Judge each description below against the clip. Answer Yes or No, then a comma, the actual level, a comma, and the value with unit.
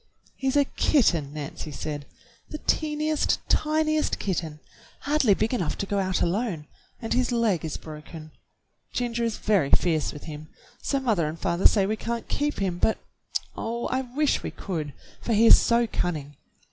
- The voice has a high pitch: Yes, high, 210 Hz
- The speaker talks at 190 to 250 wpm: No, average, 170 wpm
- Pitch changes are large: Yes, wide, 7.7 semitones